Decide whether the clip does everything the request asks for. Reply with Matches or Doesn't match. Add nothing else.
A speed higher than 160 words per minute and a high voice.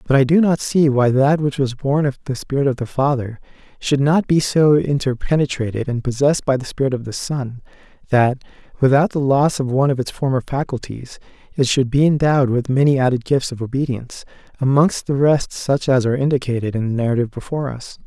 Doesn't match